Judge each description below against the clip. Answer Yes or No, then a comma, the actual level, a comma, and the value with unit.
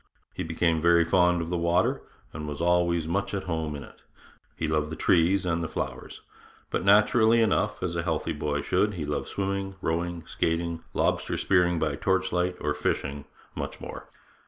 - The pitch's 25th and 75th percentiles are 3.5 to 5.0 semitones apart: No, narrow, 2.4 semitones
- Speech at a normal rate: Yes, average, 180 wpm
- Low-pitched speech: Yes, very low, 85 Hz